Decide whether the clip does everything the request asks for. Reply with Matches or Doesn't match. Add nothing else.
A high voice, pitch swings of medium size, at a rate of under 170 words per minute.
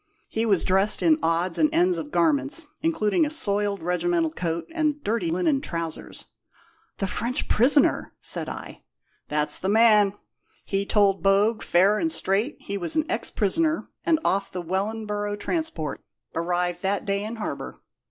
Doesn't match